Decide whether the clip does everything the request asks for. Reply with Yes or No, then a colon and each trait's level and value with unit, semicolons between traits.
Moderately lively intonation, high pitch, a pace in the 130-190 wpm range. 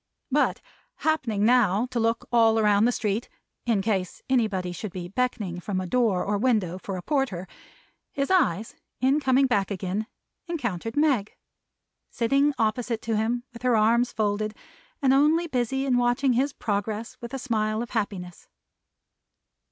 Yes: average, 3.8 semitones; high, 225 Hz; average, 155 wpm